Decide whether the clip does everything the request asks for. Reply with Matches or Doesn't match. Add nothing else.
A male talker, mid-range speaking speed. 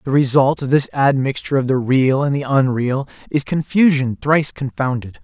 Matches